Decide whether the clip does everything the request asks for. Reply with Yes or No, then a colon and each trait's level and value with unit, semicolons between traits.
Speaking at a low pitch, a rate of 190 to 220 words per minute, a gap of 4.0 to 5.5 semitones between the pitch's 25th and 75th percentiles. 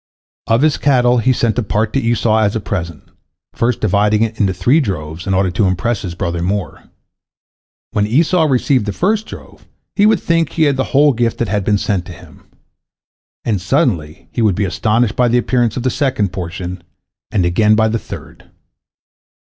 Yes: low, 110 Hz; average, 195 wpm; average, 4.6 semitones